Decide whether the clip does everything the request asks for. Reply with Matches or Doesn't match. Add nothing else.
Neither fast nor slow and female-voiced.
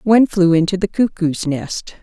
Matches